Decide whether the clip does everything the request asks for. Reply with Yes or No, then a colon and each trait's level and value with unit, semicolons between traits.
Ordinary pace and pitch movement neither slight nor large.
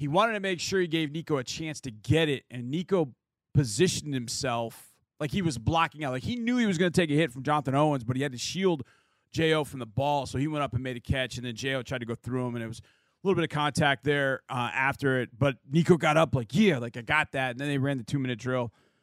No: fast, 285 wpm; average, 4.0 semitones